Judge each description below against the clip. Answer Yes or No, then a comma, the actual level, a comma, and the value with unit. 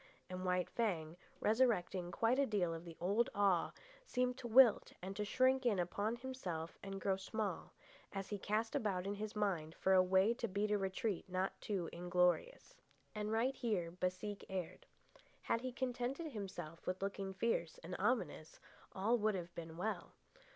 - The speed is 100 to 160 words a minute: No, average, 170 wpm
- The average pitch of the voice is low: No, high, 200 Hz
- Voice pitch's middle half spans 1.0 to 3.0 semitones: No, average, 3.9 semitones